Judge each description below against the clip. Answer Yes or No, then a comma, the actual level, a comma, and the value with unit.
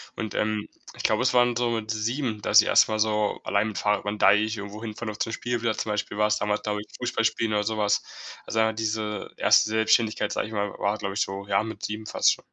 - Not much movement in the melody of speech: Yes, narrow, 1.2 semitones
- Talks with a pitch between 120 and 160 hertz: No, low, 110 Hz